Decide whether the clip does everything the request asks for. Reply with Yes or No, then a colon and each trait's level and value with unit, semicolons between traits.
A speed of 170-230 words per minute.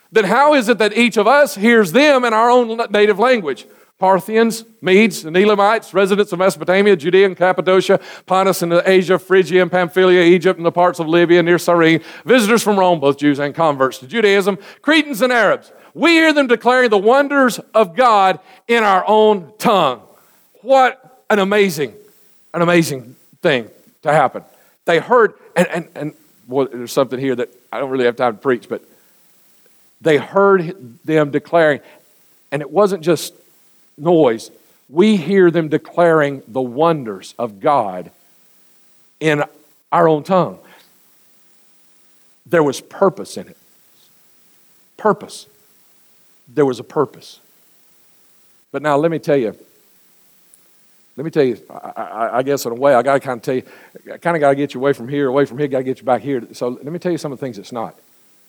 Yes: average, 175 wpm